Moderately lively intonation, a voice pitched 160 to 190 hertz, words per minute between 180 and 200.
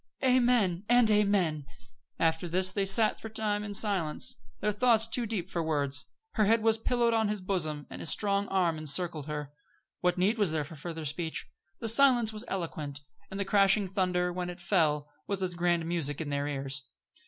Yes: average, 4.8 semitones; medium, 185 Hz; average, 195 wpm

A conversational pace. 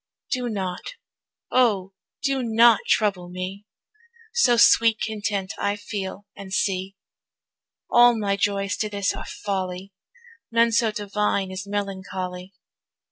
No: slow, 120 wpm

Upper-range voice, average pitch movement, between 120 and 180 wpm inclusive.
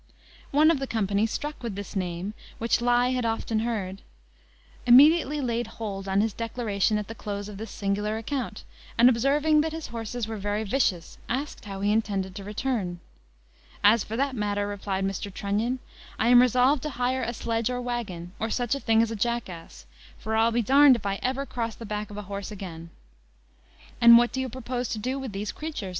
No: high, 225 Hz; average, 3.6 semitones; fast, 205 wpm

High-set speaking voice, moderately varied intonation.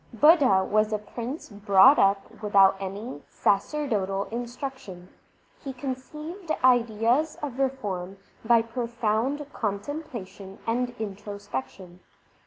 Yes: high, 225 Hz; average, 4.9 semitones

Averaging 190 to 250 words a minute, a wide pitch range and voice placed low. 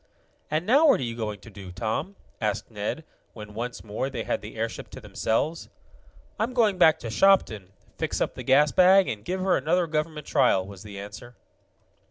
Yes: average, 195 wpm; wide, 9.0 semitones; low, 120 Hz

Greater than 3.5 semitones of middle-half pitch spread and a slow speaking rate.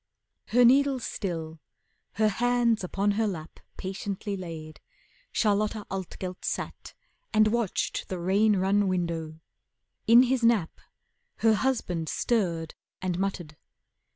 Yes: average, 4.2 semitones; slow, 115 wpm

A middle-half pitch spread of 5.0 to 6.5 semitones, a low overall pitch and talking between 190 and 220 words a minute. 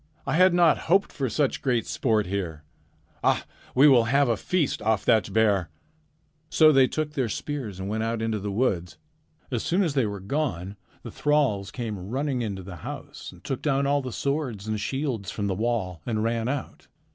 Yes: wide, 5.5 semitones; low, 115 Hz; average, 195 wpm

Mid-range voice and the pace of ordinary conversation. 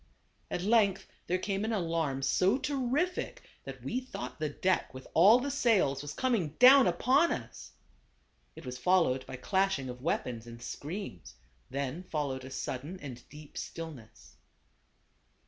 Yes: medium, 170 Hz; average, 145 wpm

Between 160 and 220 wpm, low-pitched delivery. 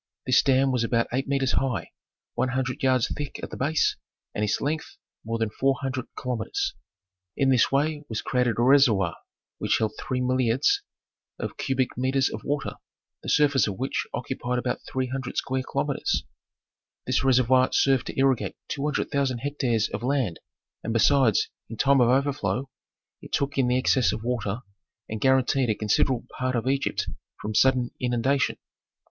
Yes: average, 170 wpm; low, 130 Hz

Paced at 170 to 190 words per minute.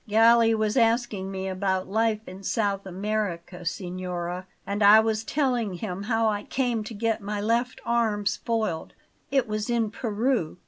No: average, 155 wpm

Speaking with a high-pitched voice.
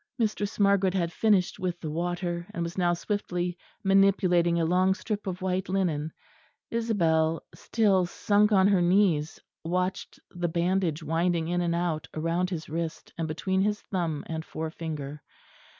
No: medium, 175 Hz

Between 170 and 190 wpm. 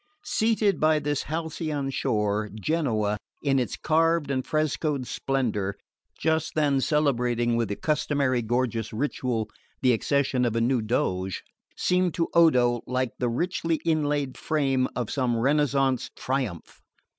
No: slow, 135 wpm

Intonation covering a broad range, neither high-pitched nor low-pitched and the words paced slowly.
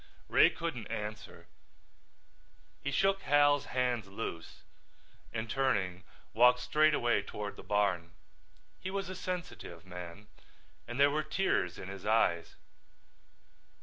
No: wide, 6.9 semitones; low, 115 Hz; slow, 120 wpm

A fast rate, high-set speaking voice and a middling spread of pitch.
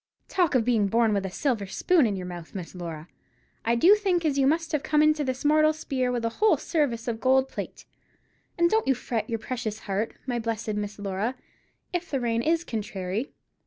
No: fast, 210 wpm; high, 240 Hz; wide, 6.2 semitones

